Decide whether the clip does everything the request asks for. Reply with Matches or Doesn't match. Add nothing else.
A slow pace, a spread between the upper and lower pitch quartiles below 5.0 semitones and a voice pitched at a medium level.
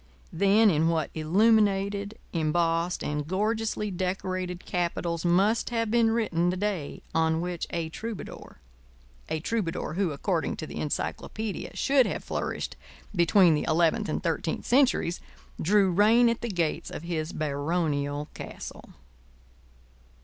Matches